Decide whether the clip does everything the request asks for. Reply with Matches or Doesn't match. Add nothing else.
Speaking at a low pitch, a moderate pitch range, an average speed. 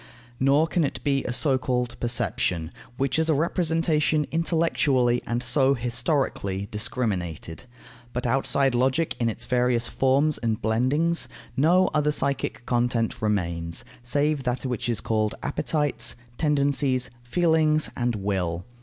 Doesn't match